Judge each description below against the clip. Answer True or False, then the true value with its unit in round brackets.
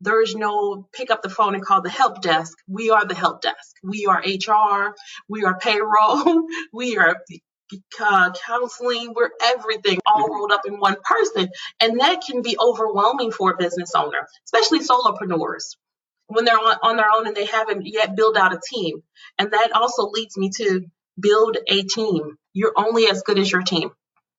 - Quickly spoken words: False (180 wpm)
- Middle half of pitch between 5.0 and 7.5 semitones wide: False (2.9 semitones)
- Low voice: False (210 Hz)